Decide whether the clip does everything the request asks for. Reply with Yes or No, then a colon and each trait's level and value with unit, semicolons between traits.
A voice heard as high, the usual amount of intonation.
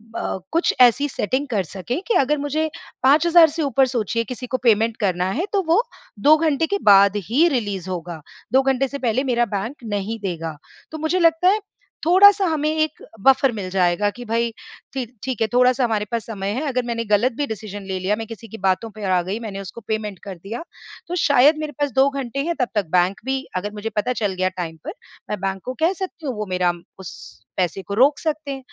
No: high, 235 Hz; wide, 6.0 semitones